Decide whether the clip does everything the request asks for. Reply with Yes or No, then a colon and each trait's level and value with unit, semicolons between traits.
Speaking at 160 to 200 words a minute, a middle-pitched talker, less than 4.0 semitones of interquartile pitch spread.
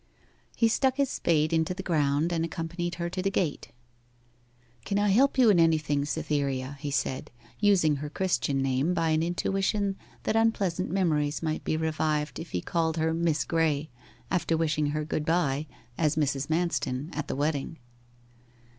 Yes: average, 165 wpm; medium, 160 Hz; average, 3.2 semitones